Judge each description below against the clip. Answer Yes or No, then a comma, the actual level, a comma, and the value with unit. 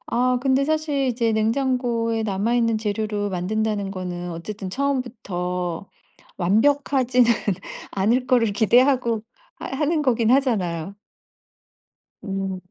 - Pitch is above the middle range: Yes, high, 225 Hz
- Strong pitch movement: No, average, 4.6 semitones